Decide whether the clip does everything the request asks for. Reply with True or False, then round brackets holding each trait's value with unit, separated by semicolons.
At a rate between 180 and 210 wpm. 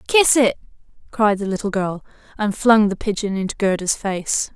False (170 wpm)